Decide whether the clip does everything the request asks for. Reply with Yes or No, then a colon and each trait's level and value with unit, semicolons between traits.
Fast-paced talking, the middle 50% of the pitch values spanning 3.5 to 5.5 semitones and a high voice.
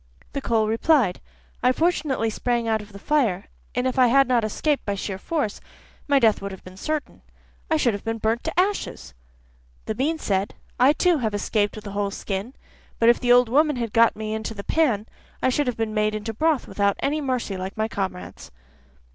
Yes: fast, 210 wpm; average, 4.8 semitones; high, 230 Hz